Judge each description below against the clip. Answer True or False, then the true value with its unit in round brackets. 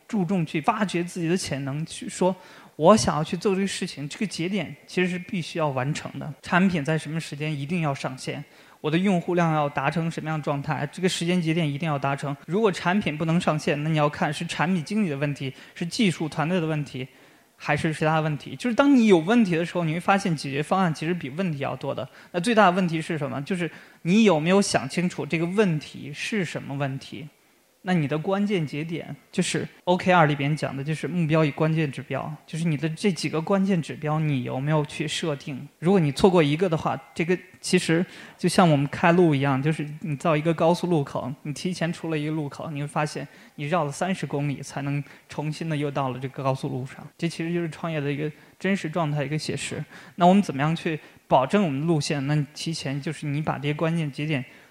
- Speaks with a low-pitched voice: False (160 Hz)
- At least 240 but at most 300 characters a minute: False (340 characters per minute)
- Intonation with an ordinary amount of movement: True (3.4 semitones)